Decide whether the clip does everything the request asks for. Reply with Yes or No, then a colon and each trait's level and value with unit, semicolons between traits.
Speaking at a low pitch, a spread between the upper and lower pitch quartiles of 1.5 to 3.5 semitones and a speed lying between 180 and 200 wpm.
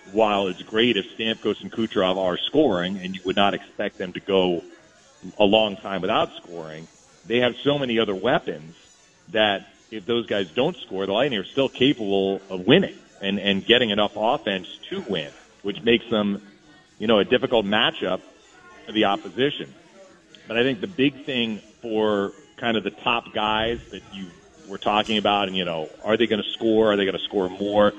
Yes: low, 105 Hz; average, 3.1 semitones; average, 195 wpm